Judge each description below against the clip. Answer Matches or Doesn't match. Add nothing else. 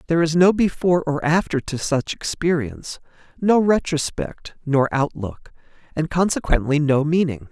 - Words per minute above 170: Doesn't match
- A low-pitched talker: Doesn't match